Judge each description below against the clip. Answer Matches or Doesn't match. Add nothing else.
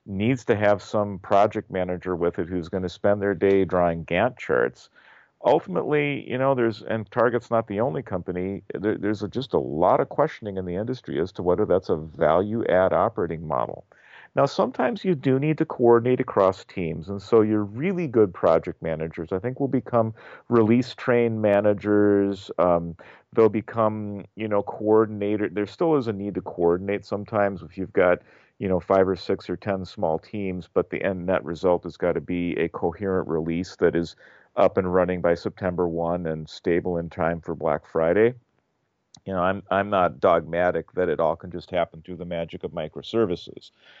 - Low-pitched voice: Matches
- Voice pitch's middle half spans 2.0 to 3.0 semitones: Doesn't match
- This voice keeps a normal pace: Matches